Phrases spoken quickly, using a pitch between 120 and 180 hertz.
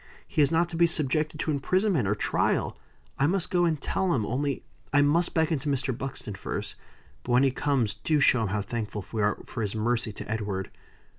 Yes: fast, 215 wpm; low, 135 Hz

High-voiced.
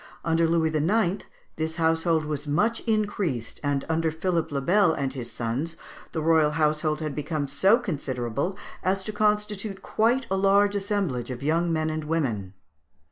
No: medium, 160 Hz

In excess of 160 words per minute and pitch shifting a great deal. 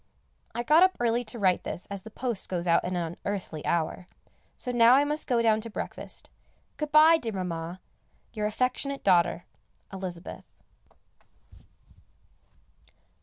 No: average, 140 wpm; wide, 5.7 semitones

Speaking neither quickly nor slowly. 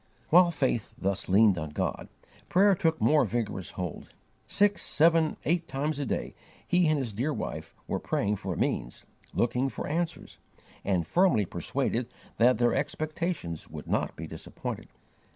Yes: average, 150 wpm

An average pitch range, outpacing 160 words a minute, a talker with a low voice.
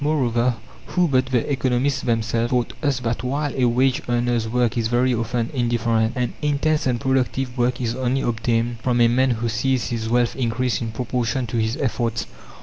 No: narrow, 1.9 semitones; average, 185 wpm; low, 120 Hz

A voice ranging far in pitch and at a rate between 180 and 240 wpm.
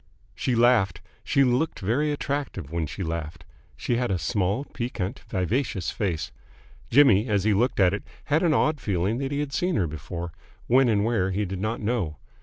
Yes: wide, 6.2 semitones; average, 190 wpm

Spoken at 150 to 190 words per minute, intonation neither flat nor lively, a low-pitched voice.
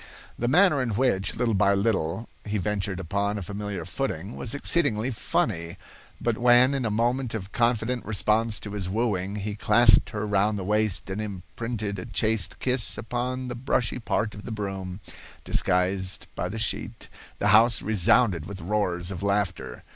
Yes: average, 170 wpm; average, 3.5 semitones; low, 105 Hz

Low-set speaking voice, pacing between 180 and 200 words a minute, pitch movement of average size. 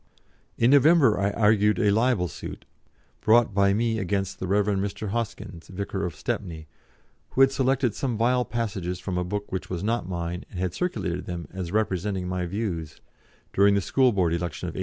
Yes: low, 100 Hz; average, 185 wpm; average, 4.2 semitones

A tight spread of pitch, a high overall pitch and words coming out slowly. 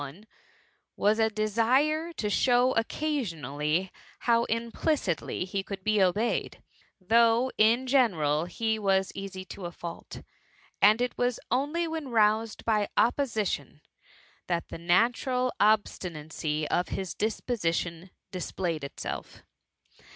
No: average, 5.1 semitones; high, 215 Hz; slow, 120 wpm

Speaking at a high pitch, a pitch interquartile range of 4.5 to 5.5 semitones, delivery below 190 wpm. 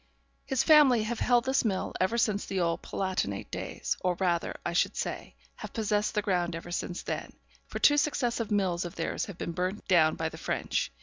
No: high, 195 Hz; average, 5.0 semitones; average, 200 wpm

